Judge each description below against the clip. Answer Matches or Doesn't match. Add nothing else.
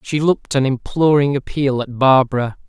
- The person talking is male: Matches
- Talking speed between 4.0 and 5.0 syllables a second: Doesn't match